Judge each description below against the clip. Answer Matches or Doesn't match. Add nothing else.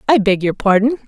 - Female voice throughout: Matches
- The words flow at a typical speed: Doesn't match